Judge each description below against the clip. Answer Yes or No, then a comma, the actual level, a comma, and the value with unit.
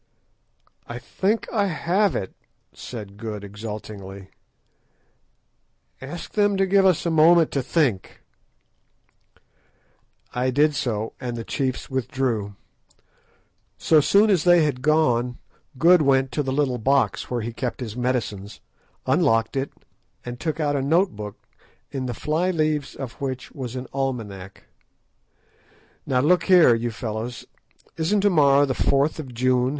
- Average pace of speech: Yes, average, 145 wpm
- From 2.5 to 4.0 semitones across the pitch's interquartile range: No, average, 5.1 semitones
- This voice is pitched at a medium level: No, low, 130 Hz